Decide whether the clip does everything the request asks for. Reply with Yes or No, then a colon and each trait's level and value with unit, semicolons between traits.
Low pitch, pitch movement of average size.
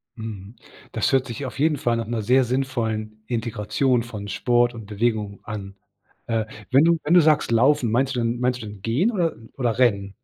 Yes: low, 120 Hz; average, 3.4 semitones